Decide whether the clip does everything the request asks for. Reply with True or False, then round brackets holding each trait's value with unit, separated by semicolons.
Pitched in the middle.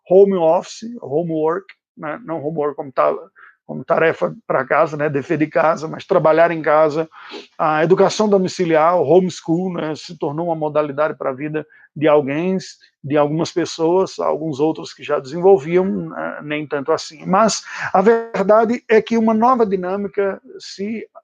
True (165 Hz)